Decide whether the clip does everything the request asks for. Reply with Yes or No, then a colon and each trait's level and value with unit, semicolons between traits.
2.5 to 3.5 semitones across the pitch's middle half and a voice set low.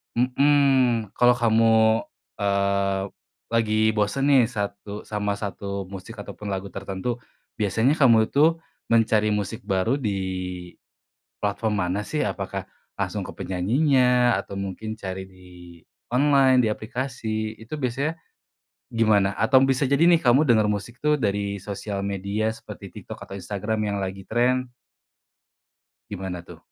No: average, 4.0 semitones; low, 110 Hz